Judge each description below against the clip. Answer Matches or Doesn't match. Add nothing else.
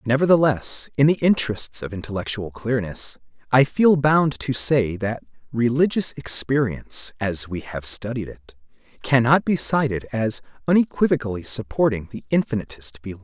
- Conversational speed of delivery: Doesn't match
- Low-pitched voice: Matches